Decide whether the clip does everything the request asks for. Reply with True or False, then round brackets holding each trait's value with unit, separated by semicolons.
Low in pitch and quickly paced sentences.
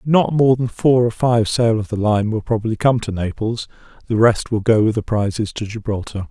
True (110 Hz; 230 wpm)